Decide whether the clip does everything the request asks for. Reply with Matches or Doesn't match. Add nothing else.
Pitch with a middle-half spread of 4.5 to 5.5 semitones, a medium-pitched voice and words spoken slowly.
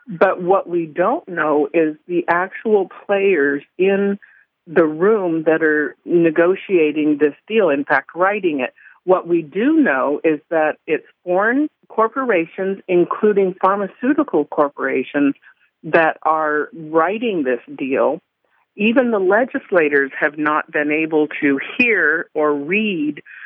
Matches